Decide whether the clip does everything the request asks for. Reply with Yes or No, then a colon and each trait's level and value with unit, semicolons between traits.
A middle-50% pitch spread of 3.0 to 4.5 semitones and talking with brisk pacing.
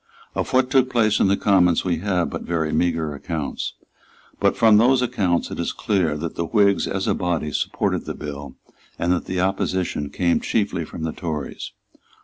No: average, 4.0 semitones; average, 180 wpm